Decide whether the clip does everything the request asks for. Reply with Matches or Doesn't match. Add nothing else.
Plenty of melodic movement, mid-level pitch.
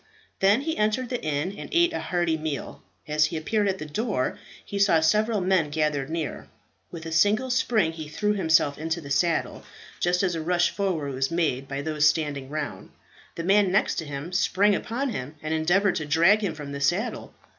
Doesn't match